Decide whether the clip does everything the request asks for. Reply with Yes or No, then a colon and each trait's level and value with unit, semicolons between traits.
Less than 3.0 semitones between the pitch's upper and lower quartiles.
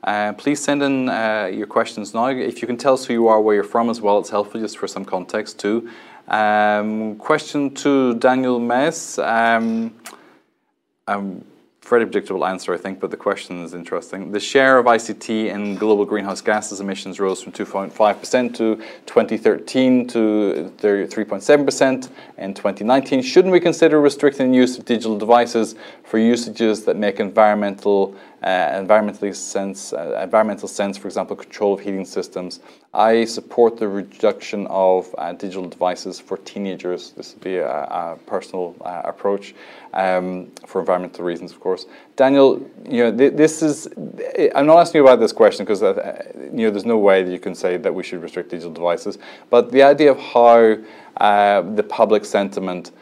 No: average, 4.4 semitones